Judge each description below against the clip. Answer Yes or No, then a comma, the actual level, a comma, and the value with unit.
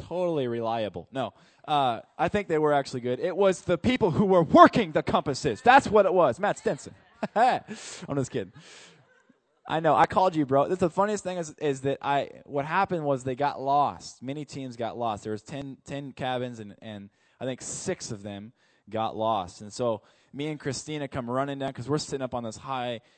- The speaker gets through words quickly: Yes, fast, 210 wpm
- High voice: No, medium, 140 Hz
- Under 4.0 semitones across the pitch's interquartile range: No, average, 5.3 semitones